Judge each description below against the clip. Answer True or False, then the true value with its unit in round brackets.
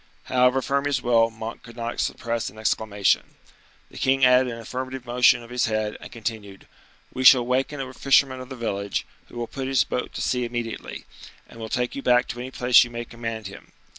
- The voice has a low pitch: True (120 Hz)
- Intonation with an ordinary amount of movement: False (2.0 semitones)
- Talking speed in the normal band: False (210 wpm)